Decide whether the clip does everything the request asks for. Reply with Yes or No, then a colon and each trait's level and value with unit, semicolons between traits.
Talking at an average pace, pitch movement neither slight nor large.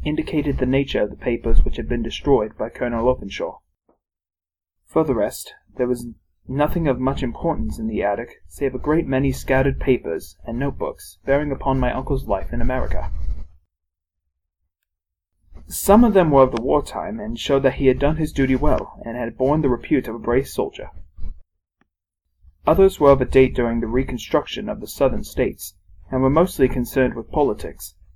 No: average, 180 wpm; wide, 7.9 semitones